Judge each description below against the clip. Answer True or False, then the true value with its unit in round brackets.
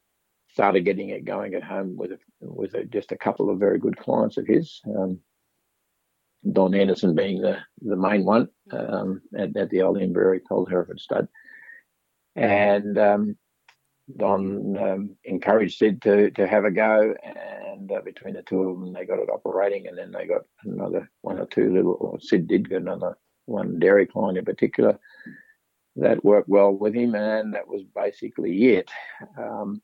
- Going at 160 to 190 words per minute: True (175 wpm)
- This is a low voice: True (105 Hz)